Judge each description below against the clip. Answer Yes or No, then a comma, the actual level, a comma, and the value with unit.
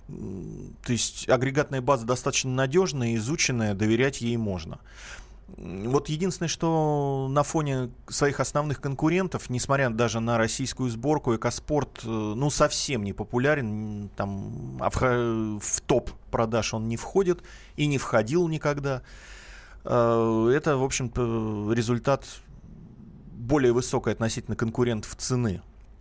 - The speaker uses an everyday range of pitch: Yes, average, 3.9 semitones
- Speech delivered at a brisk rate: No, slow, 110 wpm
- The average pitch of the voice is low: Yes, low, 125 Hz